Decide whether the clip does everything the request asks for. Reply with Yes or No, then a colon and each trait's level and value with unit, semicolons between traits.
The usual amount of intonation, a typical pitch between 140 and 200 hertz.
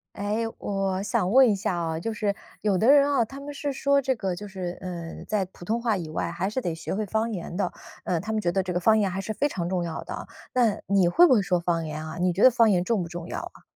Yes: average, 4.2 semitones; high, 195 Hz